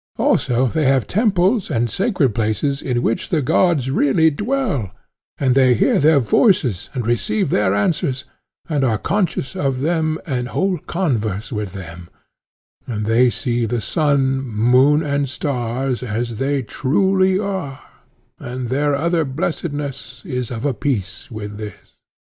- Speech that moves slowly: No, average, 145 wpm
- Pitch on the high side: No, low, 135 Hz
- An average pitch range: Yes, average, 4.9 semitones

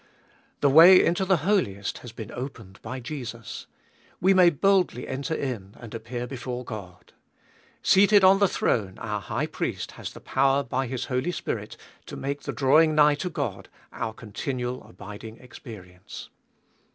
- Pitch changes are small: No, wide, 5.5 semitones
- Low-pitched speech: Yes, low, 130 Hz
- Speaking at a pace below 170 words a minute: Yes, average, 155 wpm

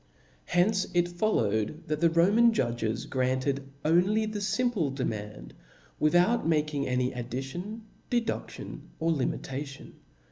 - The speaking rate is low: Yes, slow, 120 wpm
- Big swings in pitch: Yes, wide, 6.9 semitones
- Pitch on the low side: No, medium, 155 Hz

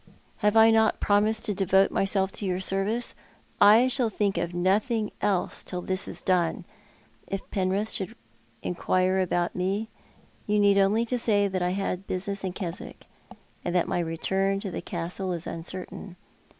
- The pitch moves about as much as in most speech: No, narrow, 2.3 semitones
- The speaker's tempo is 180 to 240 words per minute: No, average, 165 wpm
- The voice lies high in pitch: Yes, high, 195 Hz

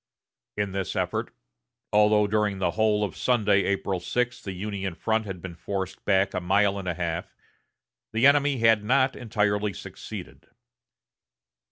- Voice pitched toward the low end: Yes, low, 105 Hz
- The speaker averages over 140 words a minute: Yes, average, 150 wpm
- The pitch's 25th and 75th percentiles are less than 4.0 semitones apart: Yes, narrow, 2.4 semitones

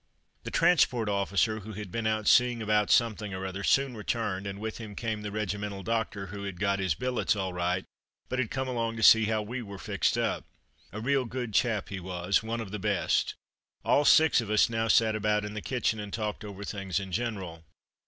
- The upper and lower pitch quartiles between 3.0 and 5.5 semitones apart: No, narrow, 2.5 semitones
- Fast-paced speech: Yes, fast, 215 wpm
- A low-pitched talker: Yes, low, 105 Hz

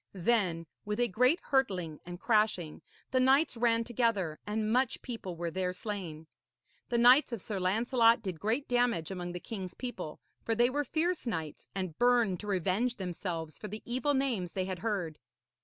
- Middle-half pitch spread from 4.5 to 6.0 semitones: Yes, average, 5.1 semitones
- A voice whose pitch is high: Yes, high, 215 Hz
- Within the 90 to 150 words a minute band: No, average, 175 wpm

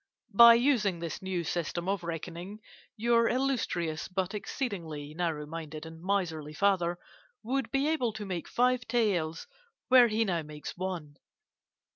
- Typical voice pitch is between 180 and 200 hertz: Yes, medium, 185 Hz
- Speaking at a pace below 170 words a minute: Yes, average, 140 wpm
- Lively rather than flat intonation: Yes, wide, 6.0 semitones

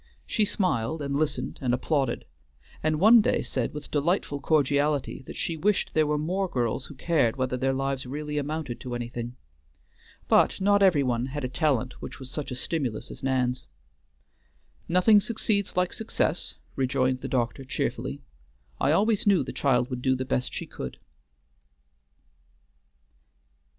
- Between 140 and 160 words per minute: Yes, average, 155 wpm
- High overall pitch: No, medium, 140 Hz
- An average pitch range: Yes, average, 4.3 semitones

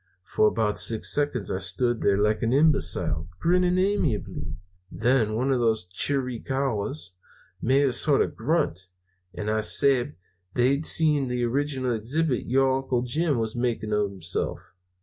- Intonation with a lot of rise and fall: No, average, 4.6 semitones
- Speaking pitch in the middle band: No, low, 120 Hz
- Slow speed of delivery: No, average, 150 wpm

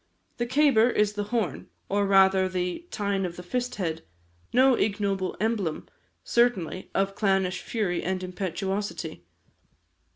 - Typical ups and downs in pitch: Yes, average, 3.0 semitones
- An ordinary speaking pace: No, slow, 130 wpm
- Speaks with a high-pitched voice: Yes, high, 195 Hz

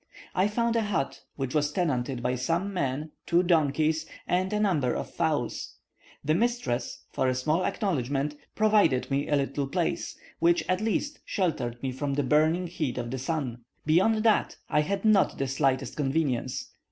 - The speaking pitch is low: No, medium, 150 Hz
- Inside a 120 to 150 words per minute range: No, average, 170 wpm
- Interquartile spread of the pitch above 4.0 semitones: Yes, wide, 5.5 semitones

